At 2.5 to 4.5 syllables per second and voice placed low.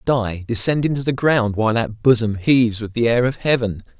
No: 5.4 syllables/s; low, 115 Hz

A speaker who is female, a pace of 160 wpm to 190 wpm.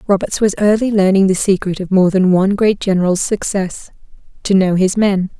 Yes: female; average, 180 wpm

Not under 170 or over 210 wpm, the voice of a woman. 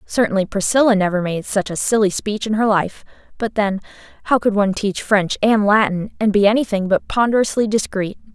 Yes: average, 185 wpm; female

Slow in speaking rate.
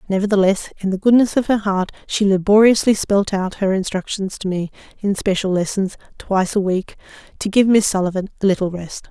No: average, 185 wpm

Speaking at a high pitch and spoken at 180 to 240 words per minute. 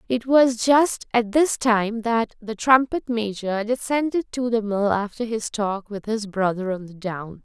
Yes: high, 225 Hz; average, 185 wpm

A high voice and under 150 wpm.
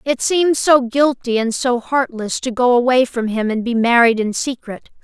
No: high, 245 Hz; fast, 205 wpm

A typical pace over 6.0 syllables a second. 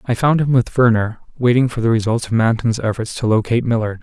Yes: 6.2 syllables/s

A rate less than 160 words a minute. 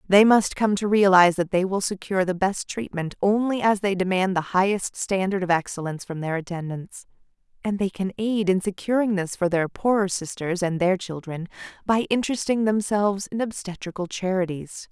No: average, 175 wpm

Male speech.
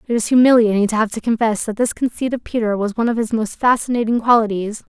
No: female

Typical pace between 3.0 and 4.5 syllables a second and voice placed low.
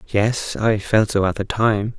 Yes: 3.8 syllables/s; low, 105 Hz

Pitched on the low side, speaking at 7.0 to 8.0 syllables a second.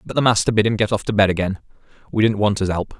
Yes: low, 105 Hz; 7.2 syllables/s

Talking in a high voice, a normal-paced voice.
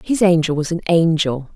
No: medium, 165 Hz; average, 190 wpm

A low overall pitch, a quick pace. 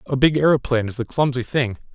Yes: low, 130 Hz; fast, 215 wpm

